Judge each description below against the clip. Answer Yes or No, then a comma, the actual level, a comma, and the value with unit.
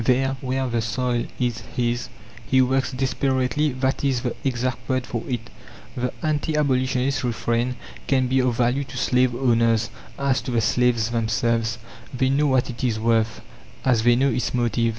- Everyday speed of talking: Yes, average, 170 wpm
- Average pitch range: No, narrow, 2.0 semitones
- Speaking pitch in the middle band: No, low, 125 Hz